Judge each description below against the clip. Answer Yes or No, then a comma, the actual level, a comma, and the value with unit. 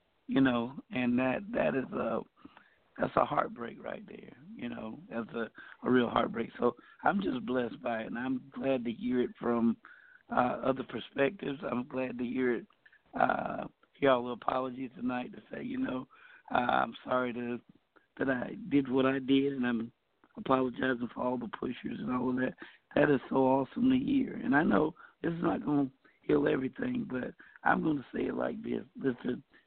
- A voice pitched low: Yes, low, 130 Hz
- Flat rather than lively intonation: Yes, narrow, 2.1 semitones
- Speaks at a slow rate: No, average, 190 wpm